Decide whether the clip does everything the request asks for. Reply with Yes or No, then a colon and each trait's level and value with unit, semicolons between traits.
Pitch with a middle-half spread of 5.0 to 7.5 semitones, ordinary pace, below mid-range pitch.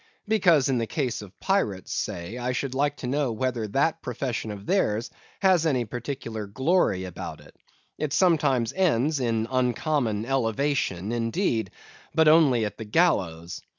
Yes: average, 5.3 semitones; average, 150 wpm; low, 125 Hz